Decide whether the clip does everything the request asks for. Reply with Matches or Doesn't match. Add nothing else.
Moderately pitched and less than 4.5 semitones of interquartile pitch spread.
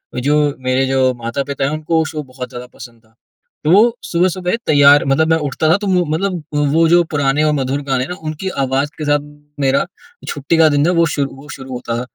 Matches